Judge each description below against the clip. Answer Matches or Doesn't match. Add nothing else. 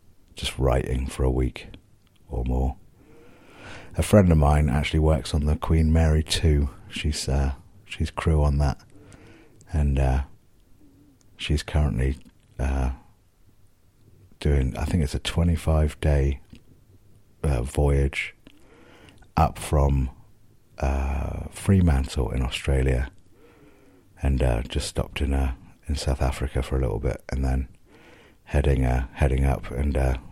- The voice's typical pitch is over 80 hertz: Doesn't match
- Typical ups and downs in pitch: Doesn't match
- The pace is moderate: Doesn't match